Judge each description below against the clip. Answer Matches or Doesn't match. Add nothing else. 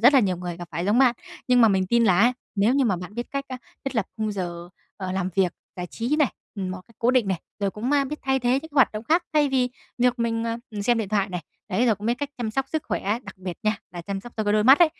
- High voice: Matches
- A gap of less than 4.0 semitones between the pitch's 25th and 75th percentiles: Doesn't match